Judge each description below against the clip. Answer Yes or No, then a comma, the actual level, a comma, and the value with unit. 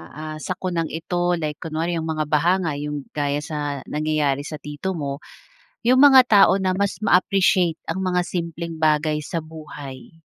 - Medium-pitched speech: Yes, medium, 160 Hz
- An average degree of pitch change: Yes, average, 3.1 semitones